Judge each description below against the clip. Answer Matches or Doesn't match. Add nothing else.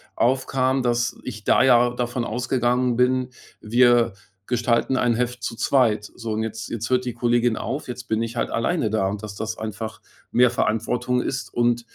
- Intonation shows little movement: Matches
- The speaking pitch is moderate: Doesn't match